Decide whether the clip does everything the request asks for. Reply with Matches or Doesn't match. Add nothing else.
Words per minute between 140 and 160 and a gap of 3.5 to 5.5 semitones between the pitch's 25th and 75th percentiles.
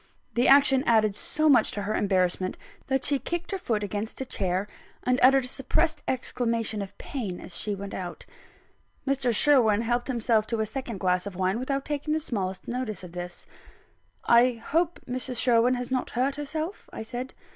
Doesn't match